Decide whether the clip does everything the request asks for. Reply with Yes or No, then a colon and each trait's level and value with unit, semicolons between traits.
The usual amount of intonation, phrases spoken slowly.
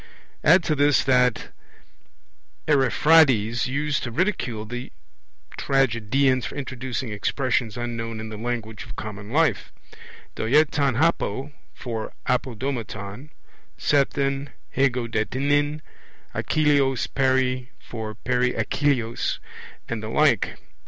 Yes: average, 3.7 semitones; slow, 105 wpm